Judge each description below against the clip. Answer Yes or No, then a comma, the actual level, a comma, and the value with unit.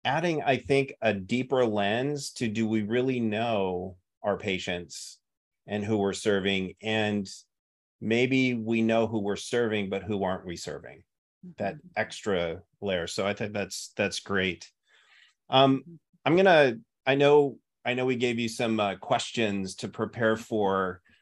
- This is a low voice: Yes, low, 110 Hz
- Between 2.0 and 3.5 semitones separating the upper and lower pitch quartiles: No, average, 4.2 semitones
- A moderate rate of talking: Yes, average, 155 wpm